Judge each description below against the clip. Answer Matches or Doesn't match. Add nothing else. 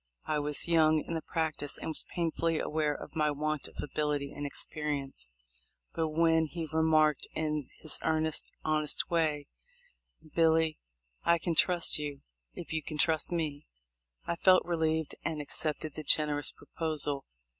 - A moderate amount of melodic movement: Doesn't match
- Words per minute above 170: Doesn't match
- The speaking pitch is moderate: Matches